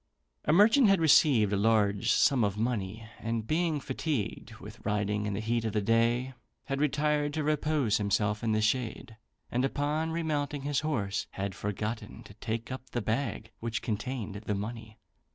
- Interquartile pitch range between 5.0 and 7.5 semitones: Yes, wide, 5.5 semitones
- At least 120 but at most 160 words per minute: No, average, 175 wpm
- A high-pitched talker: No, low, 115 Hz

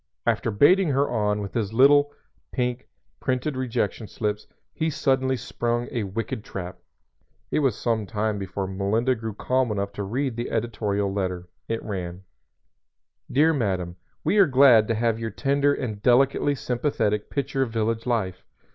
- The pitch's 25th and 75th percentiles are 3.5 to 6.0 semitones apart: Yes, average, 4.2 semitones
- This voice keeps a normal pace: Yes, average, 155 wpm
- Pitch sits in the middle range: No, low, 115 Hz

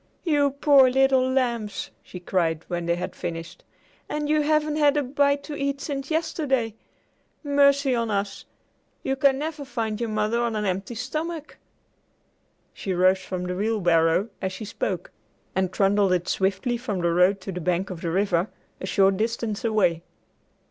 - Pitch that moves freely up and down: Yes, wide, 6.8 semitones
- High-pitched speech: Yes, high, 220 Hz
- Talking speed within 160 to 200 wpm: Yes, average, 170 wpm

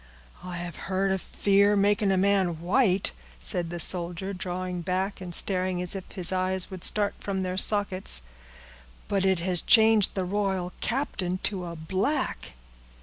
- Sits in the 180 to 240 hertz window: Yes, medium, 185 Hz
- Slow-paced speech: No, average, 160 wpm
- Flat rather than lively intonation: Yes, narrow, 1.9 semitones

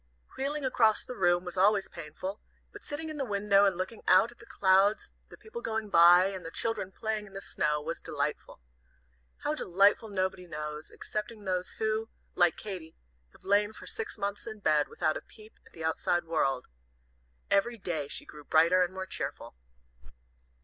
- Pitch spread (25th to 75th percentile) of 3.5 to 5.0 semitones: Yes, average, 3.9 semitones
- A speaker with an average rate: Yes, average, 180 wpm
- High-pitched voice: Yes, high, 195 Hz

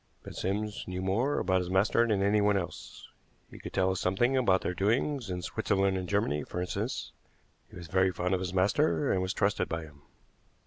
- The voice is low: Yes, very low, 95 Hz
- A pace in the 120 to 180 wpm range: No, fast, 205 wpm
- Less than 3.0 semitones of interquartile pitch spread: Yes, narrow, 2.4 semitones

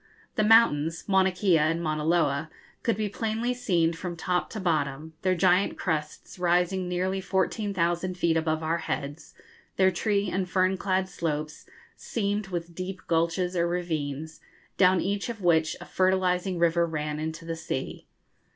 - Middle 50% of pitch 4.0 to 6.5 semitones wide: No, average, 2.7 semitones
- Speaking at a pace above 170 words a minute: No, average, 155 wpm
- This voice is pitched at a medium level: Yes, medium, 175 Hz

